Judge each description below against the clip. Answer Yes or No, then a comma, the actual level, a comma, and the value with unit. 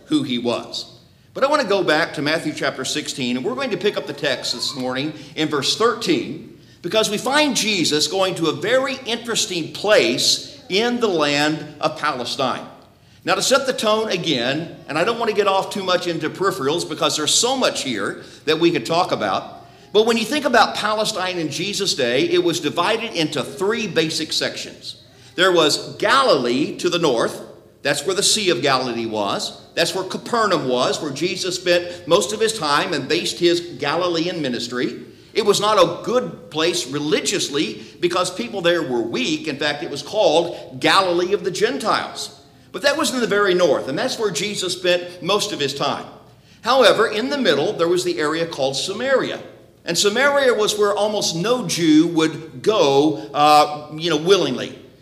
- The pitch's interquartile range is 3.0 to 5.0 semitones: No, wide, 5.6 semitones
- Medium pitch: Yes, medium, 170 Hz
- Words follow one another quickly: No, average, 190 wpm